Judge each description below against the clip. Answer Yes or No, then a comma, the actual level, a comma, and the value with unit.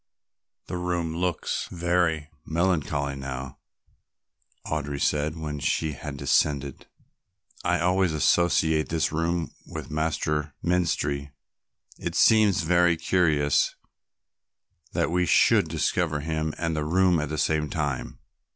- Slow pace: Yes, slow, 115 wpm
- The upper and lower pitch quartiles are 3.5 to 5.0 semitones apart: No, average, 2.8 semitones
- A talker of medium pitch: No, very low, 80 Hz